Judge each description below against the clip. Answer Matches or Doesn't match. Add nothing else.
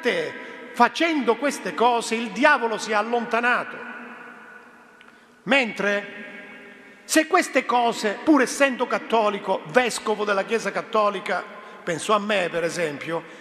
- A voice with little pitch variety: Doesn't match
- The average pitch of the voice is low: Doesn't match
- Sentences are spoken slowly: Matches